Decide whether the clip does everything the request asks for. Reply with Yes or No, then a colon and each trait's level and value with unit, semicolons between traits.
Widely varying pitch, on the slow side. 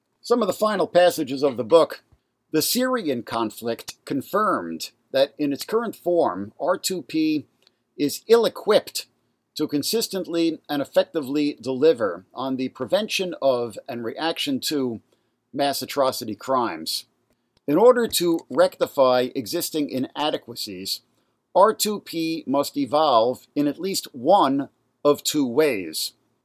Yes: wide, 7.0 semitones; slow, 120 wpm